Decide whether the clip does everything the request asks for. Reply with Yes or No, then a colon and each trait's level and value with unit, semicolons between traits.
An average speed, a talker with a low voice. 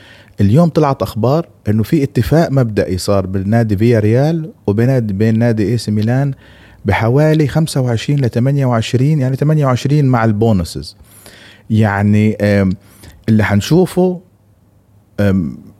Yes: average, 110 wpm; low, 115 Hz